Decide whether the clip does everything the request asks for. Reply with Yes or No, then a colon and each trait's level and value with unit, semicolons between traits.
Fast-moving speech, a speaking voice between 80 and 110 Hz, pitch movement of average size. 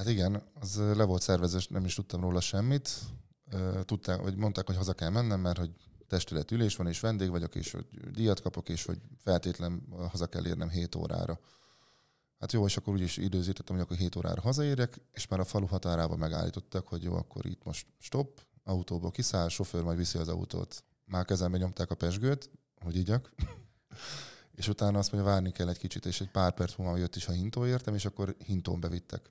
Yes: fast, 195 wpm; very low, 95 Hz; average, 3.0 semitones